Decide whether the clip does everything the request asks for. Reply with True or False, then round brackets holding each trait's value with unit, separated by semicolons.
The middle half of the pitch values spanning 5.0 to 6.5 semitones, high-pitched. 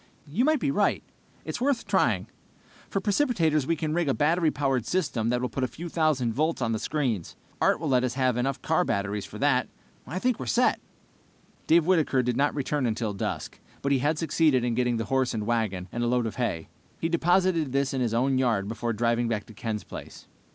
False (5.3 semitones; 130 Hz)